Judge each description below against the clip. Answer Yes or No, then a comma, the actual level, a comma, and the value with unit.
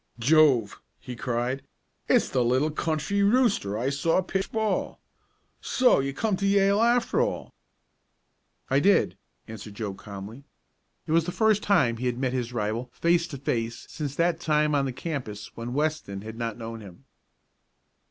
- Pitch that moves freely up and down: Yes, wide, 6.6 semitones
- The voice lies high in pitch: No, low, 135 Hz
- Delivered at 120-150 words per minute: No, average, 160 wpm